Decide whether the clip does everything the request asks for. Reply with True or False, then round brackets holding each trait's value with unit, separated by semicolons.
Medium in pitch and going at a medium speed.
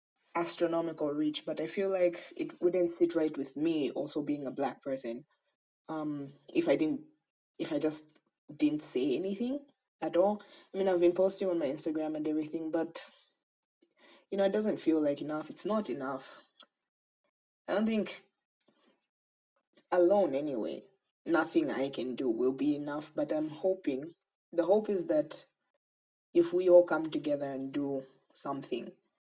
True (180 Hz; 160 wpm)